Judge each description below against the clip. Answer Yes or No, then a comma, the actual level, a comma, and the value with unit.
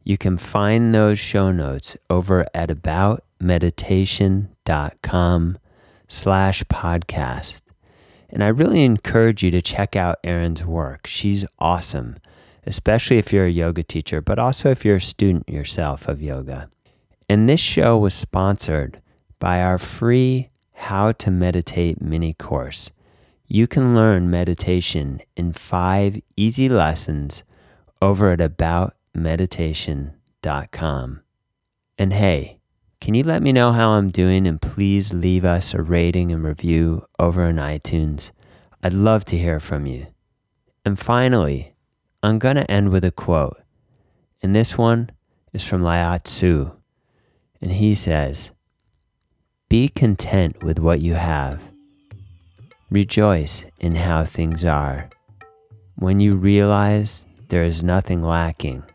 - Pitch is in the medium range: No, very low, 90 Hz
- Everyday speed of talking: No, slow, 130 wpm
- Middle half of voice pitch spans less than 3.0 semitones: No, average, 3.8 semitones